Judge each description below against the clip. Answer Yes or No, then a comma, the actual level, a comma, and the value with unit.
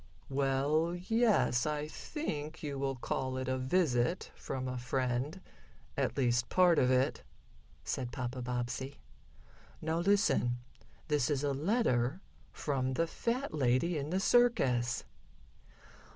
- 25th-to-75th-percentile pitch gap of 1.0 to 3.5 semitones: No, average, 4.7 semitones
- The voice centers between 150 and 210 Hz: No, medium, 140 Hz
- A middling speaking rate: No, slow, 125 wpm